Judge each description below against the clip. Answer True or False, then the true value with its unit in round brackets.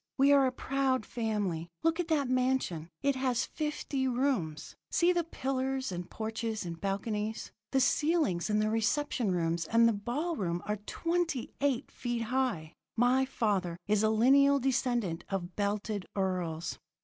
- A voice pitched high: True (230 Hz)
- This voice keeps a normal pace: True (155 wpm)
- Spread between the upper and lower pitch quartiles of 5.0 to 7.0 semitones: True (5.5 semitones)